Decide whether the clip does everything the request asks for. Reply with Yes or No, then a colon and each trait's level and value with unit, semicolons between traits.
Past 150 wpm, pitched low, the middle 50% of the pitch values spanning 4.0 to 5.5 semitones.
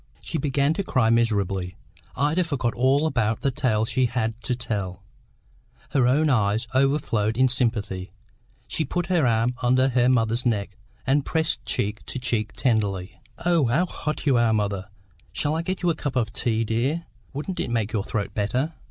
Yes: average, 180 wpm; low, 125 Hz; average, 4.5 semitones